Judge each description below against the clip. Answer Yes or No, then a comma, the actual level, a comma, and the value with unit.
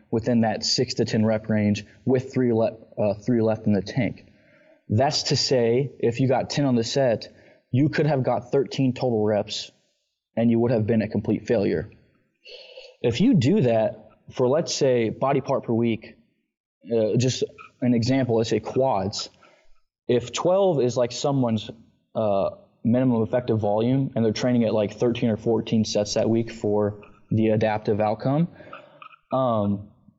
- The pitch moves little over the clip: No, average, 3.2 semitones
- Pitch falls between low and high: No, low, 115 Hz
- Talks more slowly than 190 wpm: Yes, average, 165 wpm